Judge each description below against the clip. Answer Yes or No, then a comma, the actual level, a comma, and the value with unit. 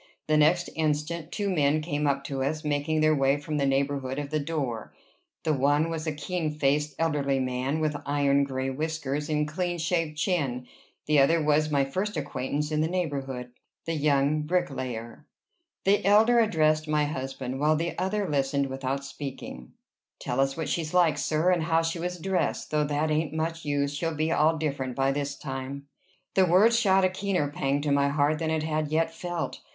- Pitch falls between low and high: Yes, medium, 150 Hz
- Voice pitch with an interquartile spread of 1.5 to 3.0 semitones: Yes, average, 2.7 semitones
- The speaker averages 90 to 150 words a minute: No, average, 190 wpm